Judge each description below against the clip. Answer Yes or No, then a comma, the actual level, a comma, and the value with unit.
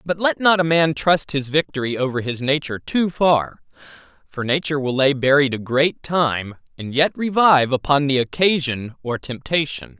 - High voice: No, medium, 145 Hz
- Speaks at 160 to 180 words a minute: Yes, average, 175 wpm